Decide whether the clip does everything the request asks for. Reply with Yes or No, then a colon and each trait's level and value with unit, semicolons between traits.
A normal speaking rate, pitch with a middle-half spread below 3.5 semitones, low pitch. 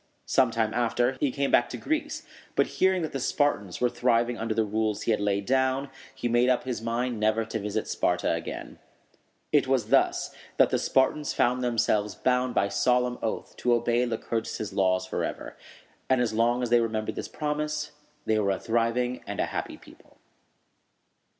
Yes: average, 180 wpm; narrow, 2.5 semitones; low, 120 Hz